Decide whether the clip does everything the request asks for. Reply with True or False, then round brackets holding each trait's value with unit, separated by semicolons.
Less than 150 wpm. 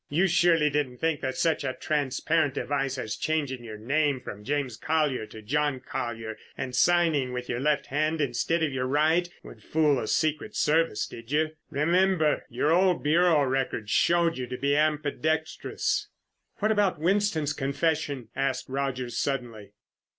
False (160 wpm)